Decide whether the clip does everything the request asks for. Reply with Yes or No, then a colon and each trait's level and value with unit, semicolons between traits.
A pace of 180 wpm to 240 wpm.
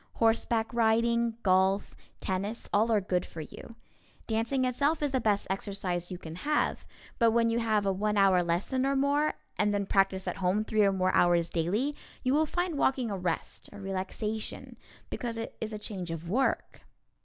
Yes: average, 185 wpm